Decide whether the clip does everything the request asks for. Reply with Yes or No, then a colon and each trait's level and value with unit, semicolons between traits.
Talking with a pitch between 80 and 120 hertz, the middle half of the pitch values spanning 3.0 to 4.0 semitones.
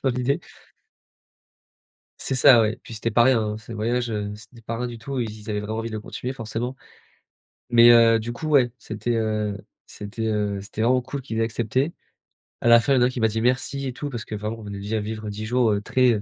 No: low, 115 Hz; narrow, 2.5 semitones